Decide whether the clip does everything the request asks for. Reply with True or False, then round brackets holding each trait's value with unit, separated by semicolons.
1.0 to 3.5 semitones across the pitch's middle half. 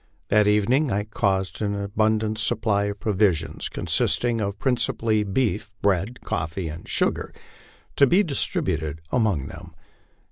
True (2.4 semitones)